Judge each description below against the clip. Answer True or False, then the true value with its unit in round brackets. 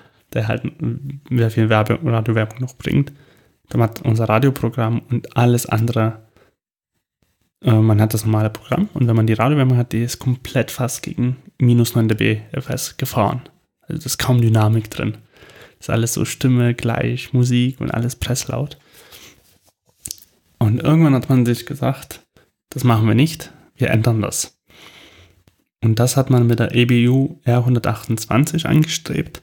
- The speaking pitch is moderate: False (120 Hz)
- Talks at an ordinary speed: True (150 wpm)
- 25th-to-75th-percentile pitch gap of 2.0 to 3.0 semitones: True (2.7 semitones)